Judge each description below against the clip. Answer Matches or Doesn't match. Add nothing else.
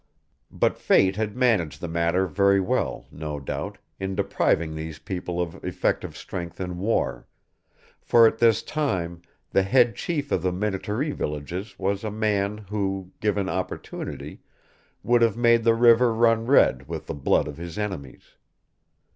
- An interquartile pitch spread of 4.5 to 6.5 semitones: Matches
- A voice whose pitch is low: Matches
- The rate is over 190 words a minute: Doesn't match